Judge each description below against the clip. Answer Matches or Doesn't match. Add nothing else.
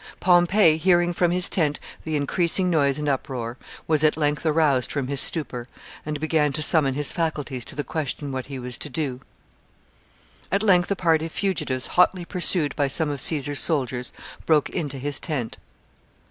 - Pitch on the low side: Doesn't match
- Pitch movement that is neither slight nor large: Matches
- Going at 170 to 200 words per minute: Matches